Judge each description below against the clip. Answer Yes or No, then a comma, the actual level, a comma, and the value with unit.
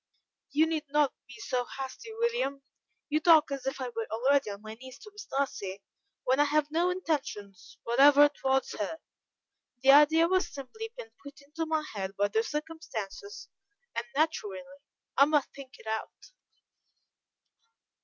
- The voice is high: Yes, very high, 280 Hz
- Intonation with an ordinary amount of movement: Yes, average, 4.5 semitones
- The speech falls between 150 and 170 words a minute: Yes, average, 155 wpm